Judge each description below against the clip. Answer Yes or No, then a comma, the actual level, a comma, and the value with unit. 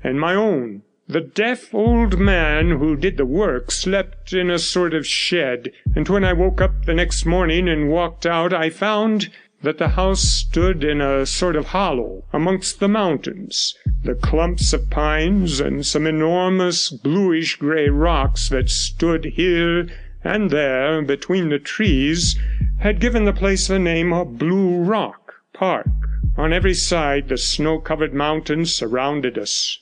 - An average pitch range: Yes, average, 3.8 semitones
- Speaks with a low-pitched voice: No, medium, 165 Hz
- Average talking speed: Yes, average, 155 wpm